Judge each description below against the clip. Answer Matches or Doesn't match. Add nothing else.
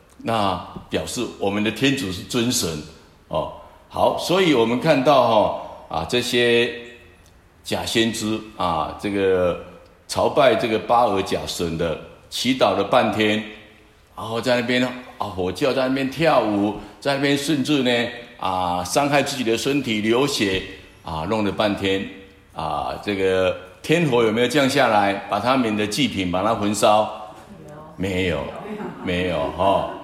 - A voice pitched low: Matches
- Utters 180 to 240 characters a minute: Matches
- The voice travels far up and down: Doesn't match